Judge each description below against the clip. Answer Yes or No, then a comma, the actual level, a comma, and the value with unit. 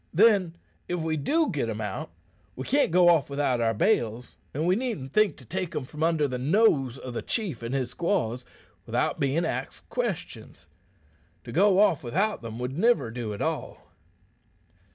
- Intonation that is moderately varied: No, wide, 7.0 semitones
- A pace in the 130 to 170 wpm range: No, average, 180 wpm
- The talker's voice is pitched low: No, medium, 150 Hz